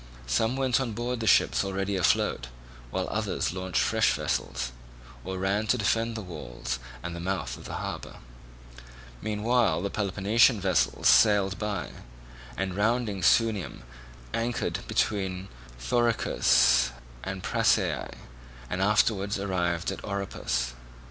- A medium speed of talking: No, slow, 125 wpm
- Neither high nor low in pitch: No, low, 100 Hz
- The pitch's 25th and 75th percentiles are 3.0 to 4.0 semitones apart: Yes, average, 3.4 semitones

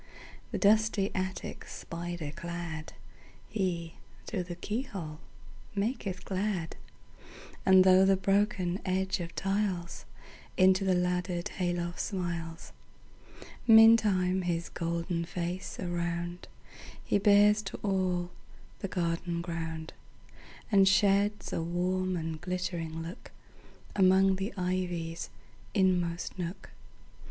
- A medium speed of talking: No, slow, 90 wpm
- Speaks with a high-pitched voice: No, medium, 180 Hz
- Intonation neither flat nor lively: No, narrow, 2.2 semitones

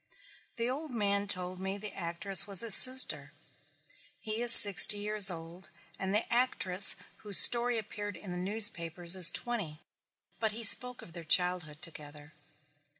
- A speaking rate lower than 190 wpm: Yes, average, 150 wpm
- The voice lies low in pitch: No, high, 200 Hz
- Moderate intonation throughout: Yes, average, 3.9 semitones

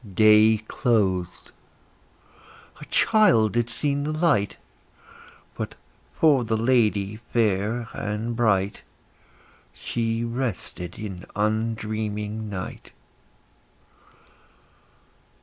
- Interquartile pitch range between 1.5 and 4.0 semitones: Yes, narrow, 2.4 semitones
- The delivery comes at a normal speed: No, slow, 80 wpm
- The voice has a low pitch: Yes, low, 110 Hz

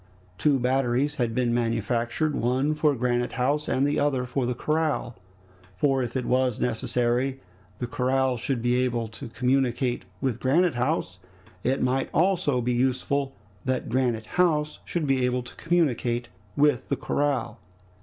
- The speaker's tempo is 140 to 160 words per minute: Yes, average, 150 wpm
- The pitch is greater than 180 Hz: No, low, 130 Hz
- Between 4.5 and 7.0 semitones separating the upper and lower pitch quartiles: No, average, 2.7 semitones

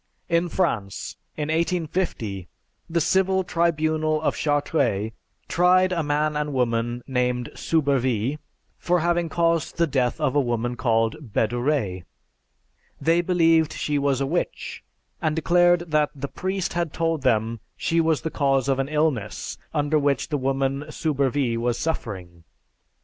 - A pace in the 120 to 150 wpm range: Yes, average, 140 wpm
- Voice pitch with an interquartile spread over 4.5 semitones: Yes, average, 4.9 semitones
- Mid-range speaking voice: Yes, medium, 145 Hz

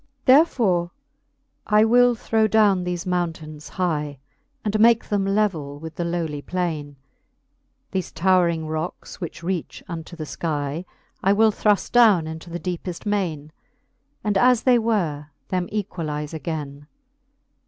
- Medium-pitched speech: Yes, medium, 175 Hz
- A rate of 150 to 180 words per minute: No, average, 140 wpm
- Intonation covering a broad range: No, average, 4.7 semitones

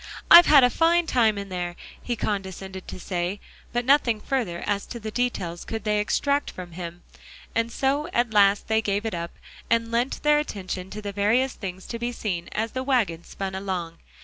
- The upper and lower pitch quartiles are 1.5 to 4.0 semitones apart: No, average, 4.5 semitones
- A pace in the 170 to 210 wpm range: Yes, average, 200 wpm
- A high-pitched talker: Yes, high, 210 Hz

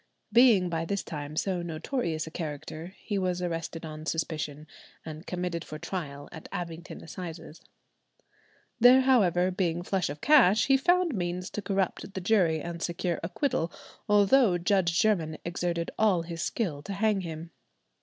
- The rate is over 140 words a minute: Yes, average, 155 wpm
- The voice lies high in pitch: No, medium, 175 Hz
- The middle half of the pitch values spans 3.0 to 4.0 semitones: Yes, average, 3.5 semitones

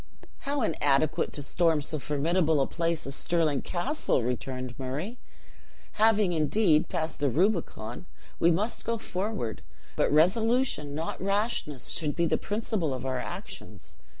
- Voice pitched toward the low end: No, medium, 165 Hz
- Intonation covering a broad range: Yes, wide, 6.2 semitones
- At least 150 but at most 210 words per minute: No, average, 140 wpm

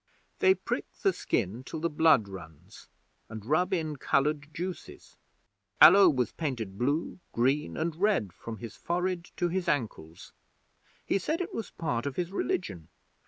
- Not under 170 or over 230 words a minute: No, average, 155 wpm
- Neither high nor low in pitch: Yes, medium, 150 Hz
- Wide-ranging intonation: Yes, wide, 7.3 semitones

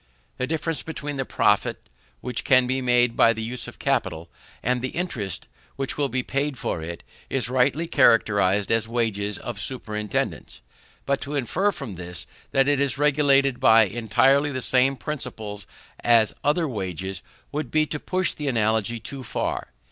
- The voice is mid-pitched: No, low, 125 Hz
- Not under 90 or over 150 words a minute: No, average, 165 wpm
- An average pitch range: Yes, average, 4.2 semitones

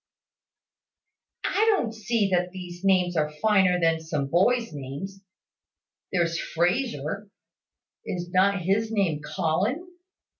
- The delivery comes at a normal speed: No, slow, 110 wpm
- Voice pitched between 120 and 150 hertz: No, medium, 185 Hz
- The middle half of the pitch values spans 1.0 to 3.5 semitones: No, average, 3.9 semitones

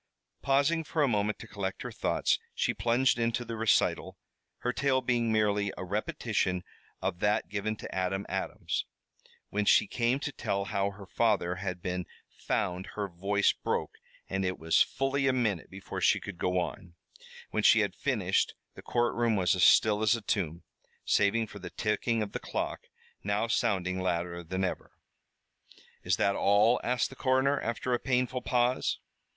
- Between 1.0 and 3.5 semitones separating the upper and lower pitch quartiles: No, average, 4.1 semitones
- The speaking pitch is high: No, low, 105 Hz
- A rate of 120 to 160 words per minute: No, average, 170 wpm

